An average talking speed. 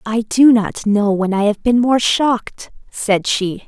Yes: average, 195 wpm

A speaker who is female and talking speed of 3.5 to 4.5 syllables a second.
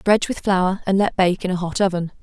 No: female; 5.9 syllables/s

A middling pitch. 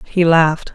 Yes: medium, 165 Hz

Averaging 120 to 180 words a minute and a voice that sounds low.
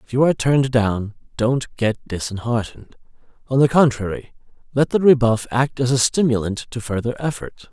Yes: average, 165 wpm; low, 125 Hz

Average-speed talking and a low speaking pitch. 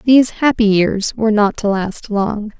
No: average, 185 wpm; high, 215 Hz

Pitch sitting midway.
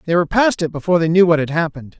Yes: medium, 170 Hz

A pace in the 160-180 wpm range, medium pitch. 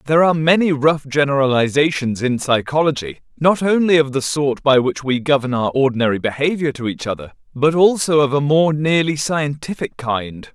Yes: average, 170 wpm; medium, 145 Hz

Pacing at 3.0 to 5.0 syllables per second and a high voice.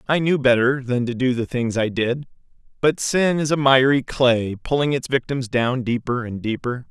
No: 4.8 syllables/s; low, 125 Hz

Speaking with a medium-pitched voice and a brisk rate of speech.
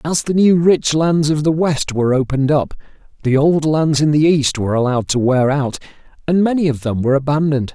Yes: medium, 145 Hz; fast, 215 wpm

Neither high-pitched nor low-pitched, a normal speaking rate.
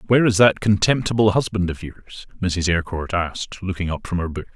No: very low, 95 Hz; average, 195 wpm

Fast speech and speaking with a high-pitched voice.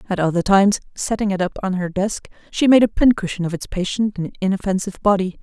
Yes: fast, 210 wpm; high, 195 Hz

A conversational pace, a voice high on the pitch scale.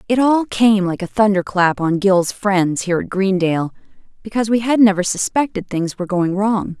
Yes: average, 185 wpm; high, 200 Hz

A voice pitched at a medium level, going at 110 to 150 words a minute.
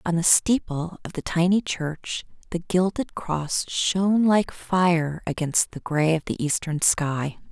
No: medium, 170 Hz; average, 160 wpm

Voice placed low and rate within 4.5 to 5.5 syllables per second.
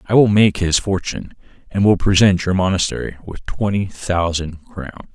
Yes: very low, 95 Hz; 5.0 syllables/s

